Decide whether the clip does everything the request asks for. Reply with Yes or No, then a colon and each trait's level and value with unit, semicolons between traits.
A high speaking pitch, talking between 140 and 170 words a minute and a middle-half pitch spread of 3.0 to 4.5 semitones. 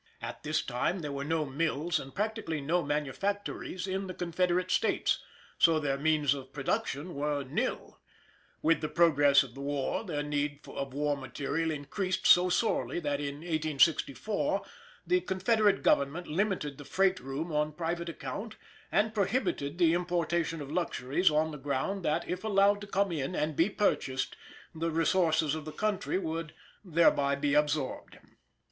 No: medium, 160 Hz; average, 160 wpm; average, 4.1 semitones